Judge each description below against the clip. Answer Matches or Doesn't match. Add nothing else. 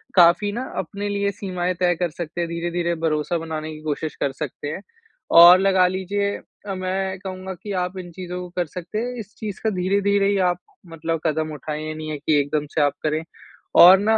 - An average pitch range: Matches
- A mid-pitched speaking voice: Matches